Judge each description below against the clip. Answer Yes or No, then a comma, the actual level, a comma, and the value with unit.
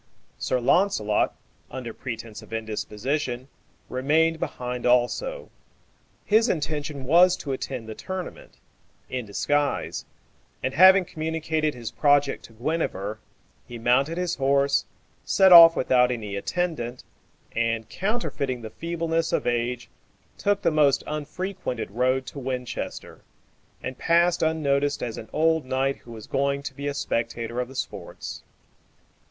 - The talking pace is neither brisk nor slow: No, slow, 130 wpm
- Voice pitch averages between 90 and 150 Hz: Yes, medium, 140 Hz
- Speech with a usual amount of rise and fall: Yes, average, 5.0 semitones